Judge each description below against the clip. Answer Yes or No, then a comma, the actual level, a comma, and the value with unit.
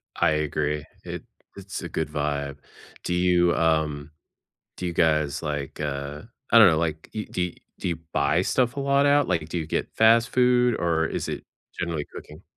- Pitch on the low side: Yes, very low, 80 Hz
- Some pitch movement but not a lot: Yes, average, 4.6 semitones